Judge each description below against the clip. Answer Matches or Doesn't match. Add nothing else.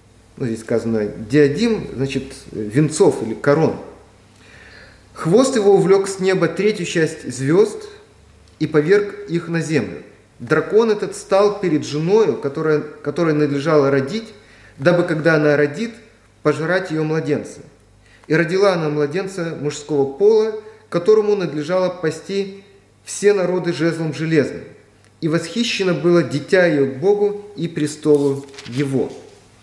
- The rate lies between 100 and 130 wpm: Matches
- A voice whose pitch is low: Doesn't match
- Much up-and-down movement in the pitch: Matches